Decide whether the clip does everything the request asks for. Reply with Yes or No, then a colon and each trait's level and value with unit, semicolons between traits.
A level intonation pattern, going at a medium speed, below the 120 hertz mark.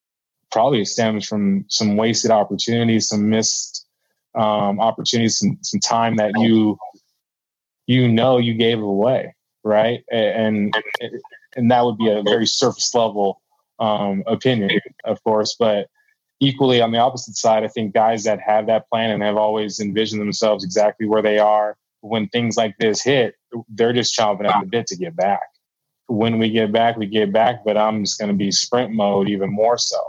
Yes: narrow, 1.6 semitones; average, 175 wpm; low, 110 Hz